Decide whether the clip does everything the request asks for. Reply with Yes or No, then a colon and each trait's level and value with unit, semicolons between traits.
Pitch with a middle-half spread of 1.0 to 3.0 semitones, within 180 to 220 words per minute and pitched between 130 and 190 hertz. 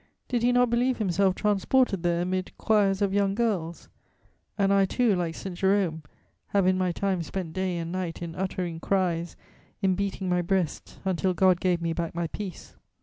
Yes: narrow, 2.5 semitones; average, 185 wpm; medium, 185 Hz